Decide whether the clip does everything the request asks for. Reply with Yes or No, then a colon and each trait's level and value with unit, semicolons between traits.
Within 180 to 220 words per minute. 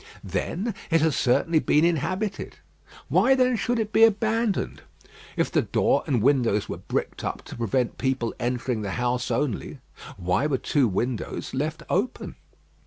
No: average, 155 wpm